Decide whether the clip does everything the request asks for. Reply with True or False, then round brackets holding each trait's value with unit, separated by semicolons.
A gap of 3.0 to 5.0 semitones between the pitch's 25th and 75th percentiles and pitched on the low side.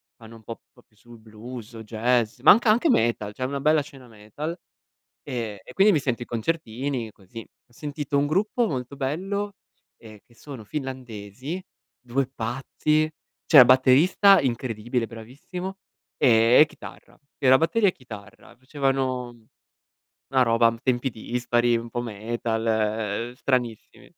True (3.8 semitones; 125 Hz)